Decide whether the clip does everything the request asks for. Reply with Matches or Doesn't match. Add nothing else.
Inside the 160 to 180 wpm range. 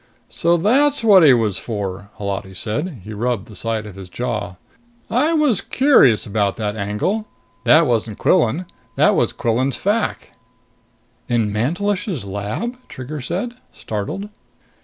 Doesn't match